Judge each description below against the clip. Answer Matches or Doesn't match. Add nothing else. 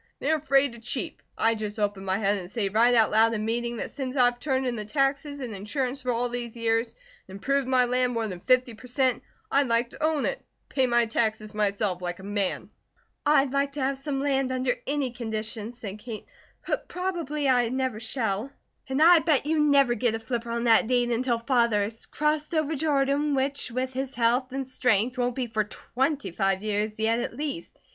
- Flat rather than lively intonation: Doesn't match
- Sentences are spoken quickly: Matches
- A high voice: Matches